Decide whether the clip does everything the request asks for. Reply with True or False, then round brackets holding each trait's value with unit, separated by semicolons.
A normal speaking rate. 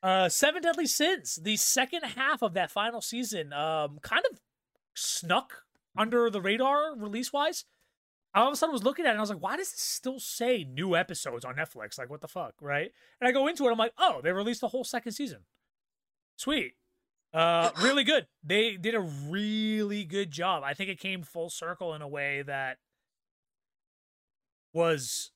True (195 wpm)